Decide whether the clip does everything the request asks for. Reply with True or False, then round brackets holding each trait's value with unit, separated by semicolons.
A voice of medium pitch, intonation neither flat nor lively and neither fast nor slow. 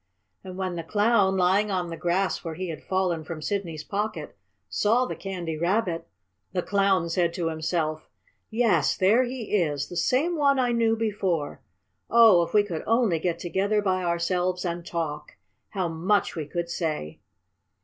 True (180 Hz; 3.7 semitones; 170 wpm)